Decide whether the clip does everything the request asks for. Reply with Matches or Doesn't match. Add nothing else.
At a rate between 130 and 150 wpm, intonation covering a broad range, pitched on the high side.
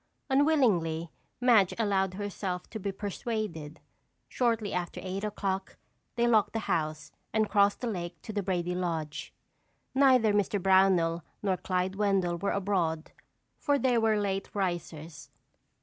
Doesn't match